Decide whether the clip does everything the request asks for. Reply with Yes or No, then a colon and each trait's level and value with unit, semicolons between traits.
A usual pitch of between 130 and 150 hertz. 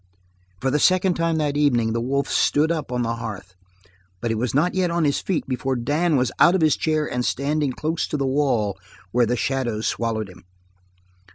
Yes: low, 135 Hz